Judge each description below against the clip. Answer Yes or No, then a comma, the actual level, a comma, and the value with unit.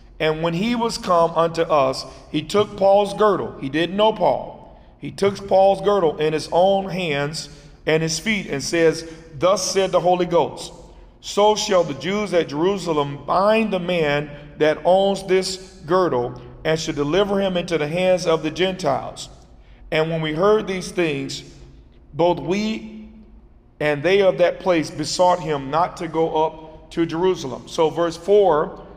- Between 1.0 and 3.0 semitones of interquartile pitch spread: No, average, 3.8 semitones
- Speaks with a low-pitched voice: No, medium, 170 Hz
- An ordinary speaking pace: Yes, average, 165 wpm